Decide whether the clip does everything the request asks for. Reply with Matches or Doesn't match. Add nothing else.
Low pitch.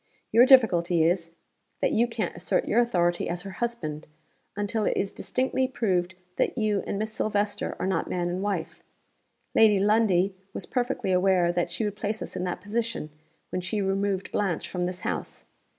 Doesn't match